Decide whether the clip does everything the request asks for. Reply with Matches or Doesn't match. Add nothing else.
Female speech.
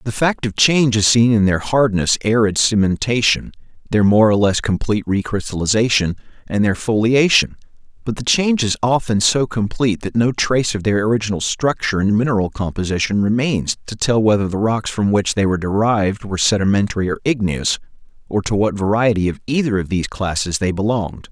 Doesn't match